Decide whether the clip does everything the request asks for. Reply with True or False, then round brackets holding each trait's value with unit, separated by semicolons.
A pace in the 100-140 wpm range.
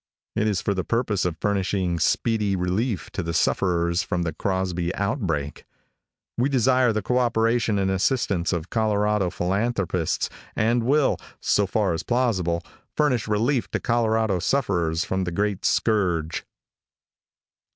True (135 wpm)